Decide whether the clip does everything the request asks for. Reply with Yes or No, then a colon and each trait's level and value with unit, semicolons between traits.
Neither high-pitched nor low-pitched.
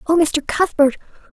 No: very high, 305 Hz